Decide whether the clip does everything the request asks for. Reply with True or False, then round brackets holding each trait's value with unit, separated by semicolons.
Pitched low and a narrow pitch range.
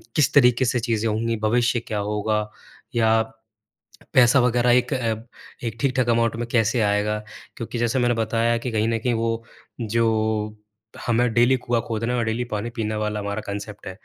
True (115 Hz; 1.9 semitones)